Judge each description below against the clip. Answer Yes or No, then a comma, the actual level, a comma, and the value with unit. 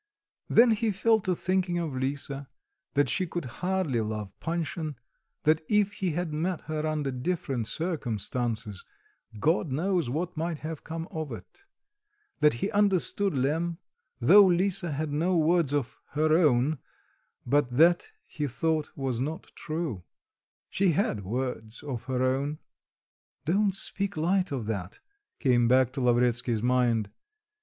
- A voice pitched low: No, medium, 155 Hz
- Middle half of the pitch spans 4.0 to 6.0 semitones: Yes, wide, 5.6 semitones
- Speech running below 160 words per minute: Yes, average, 140 wpm